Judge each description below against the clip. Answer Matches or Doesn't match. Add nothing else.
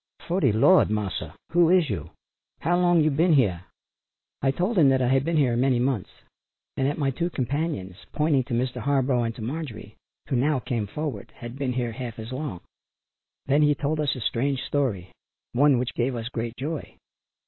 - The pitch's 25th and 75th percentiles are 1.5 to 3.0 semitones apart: Doesn't match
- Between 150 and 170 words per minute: Doesn't match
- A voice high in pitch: Doesn't match